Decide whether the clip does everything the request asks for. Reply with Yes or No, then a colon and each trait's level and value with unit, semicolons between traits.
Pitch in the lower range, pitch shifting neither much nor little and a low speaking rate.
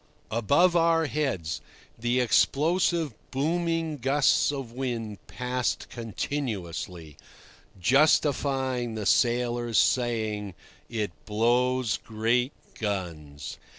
Yes: low, 120 Hz; average, 4.6 semitones; slow, 85 wpm